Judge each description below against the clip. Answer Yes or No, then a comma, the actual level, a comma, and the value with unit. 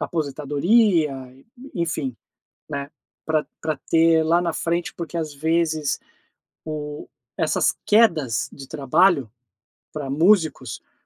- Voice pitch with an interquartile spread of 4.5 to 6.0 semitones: No, average, 2.9 semitones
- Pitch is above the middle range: No, medium, 160 Hz